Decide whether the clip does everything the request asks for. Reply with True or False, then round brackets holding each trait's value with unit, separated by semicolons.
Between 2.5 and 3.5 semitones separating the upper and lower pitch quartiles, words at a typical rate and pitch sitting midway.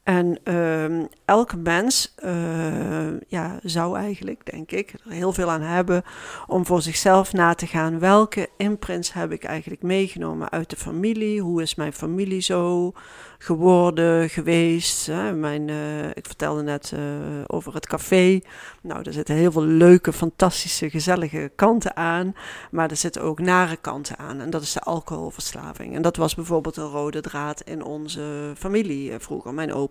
True (2.9 semitones; 165 wpm; 165 Hz)